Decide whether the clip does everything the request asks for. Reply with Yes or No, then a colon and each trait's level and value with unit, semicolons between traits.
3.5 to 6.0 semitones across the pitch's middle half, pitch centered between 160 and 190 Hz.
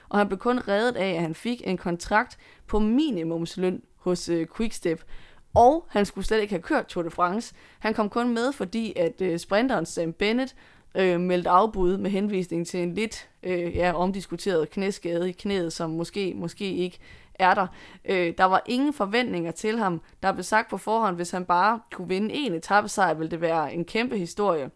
Yes: average, 3.9 semitones; medium, 185 Hz